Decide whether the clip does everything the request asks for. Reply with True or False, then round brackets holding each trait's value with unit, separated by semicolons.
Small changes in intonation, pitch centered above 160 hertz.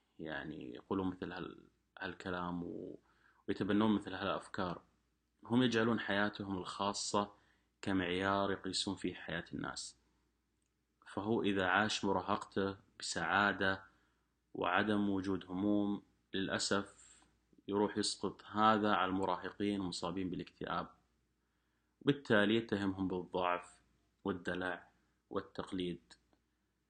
False (2.2 semitones; 95 Hz)